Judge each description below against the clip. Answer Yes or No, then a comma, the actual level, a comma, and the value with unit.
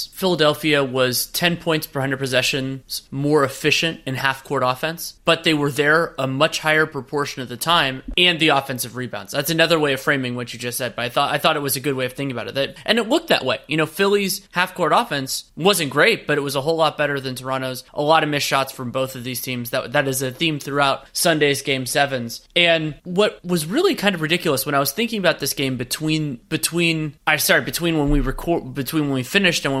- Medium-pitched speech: Yes, medium, 145 Hz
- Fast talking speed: Yes, fast, 245 wpm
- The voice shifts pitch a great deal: No, average, 3.5 semitones